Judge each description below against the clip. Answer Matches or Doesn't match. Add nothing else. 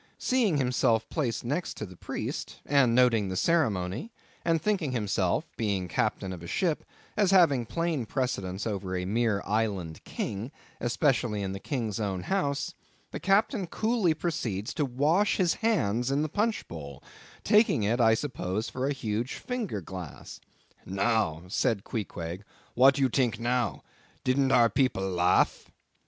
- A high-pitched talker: Doesn't match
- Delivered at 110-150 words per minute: Matches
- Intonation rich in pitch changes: Matches